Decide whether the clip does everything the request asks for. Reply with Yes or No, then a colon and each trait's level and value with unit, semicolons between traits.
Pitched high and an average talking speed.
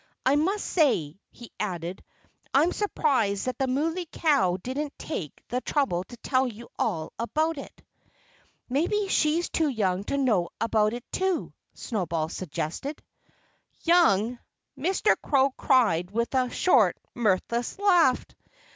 No: very high, 255 Hz; slow, 130 wpm